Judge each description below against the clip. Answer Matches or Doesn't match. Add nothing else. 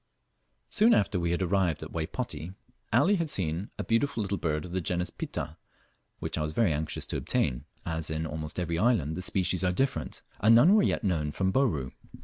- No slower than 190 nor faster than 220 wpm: Matches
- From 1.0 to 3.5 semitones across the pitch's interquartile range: Doesn't match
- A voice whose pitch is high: Doesn't match